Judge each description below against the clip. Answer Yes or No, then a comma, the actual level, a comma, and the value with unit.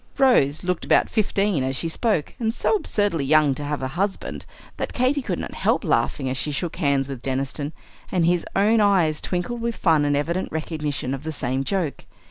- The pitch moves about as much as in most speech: No, wide, 6.0 semitones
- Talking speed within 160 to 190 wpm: No, average, 200 wpm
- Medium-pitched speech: Yes, medium, 160 Hz